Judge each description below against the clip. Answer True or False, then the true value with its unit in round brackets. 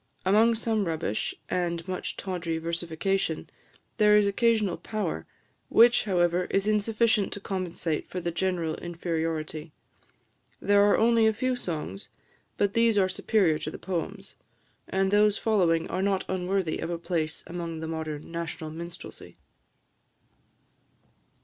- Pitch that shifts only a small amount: False (3.8 semitones)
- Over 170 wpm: False (135 wpm)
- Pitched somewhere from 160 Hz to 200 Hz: True (185 Hz)